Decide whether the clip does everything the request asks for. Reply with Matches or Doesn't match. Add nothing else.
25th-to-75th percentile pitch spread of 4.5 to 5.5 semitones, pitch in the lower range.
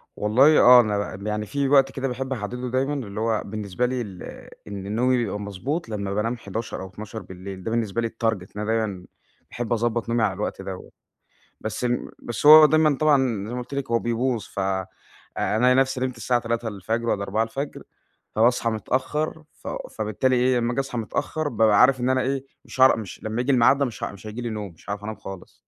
Doesn't match